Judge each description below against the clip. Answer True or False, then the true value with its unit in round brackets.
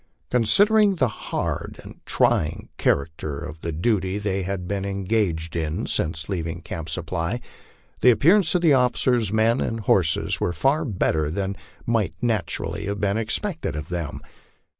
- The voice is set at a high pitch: False (100 Hz)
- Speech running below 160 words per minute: True (150 wpm)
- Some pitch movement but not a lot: False (6.1 semitones)